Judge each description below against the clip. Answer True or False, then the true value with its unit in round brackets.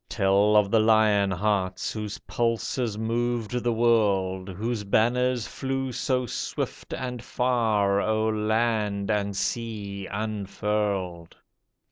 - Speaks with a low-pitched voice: True (110 Hz)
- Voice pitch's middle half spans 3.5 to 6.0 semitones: False (2.7 semitones)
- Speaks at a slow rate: True (110 wpm)